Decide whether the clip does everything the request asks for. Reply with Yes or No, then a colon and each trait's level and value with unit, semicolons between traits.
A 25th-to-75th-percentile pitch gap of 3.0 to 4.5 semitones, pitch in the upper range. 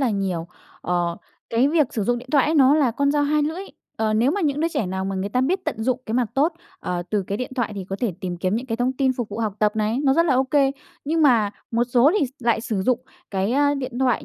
No: average, 5.0 semitones; high, 245 Hz